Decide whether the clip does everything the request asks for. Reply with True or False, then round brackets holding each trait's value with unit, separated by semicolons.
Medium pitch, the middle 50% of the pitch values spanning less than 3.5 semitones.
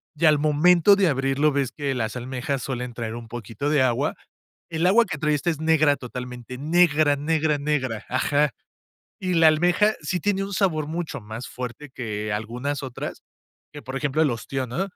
False (145 Hz; 4.2 semitones)